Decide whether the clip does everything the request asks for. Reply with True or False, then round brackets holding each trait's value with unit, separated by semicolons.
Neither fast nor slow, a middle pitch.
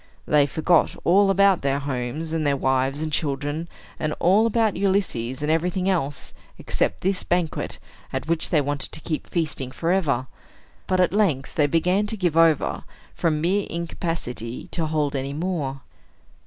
True (160 wpm; 160 Hz)